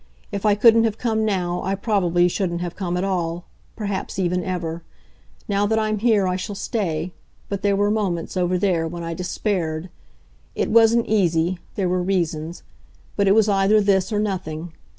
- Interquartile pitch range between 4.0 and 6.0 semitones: No, average, 2.9 semitones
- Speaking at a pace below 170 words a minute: No, average, 180 wpm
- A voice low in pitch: No, high, 190 Hz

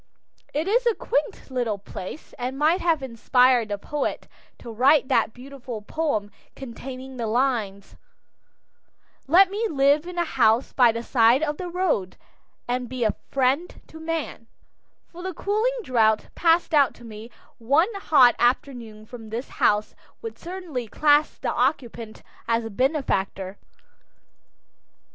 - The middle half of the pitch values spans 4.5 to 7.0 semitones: Yes, wide, 5.6 semitones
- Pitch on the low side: No, very high, 260 Hz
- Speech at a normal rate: Yes, average, 145 wpm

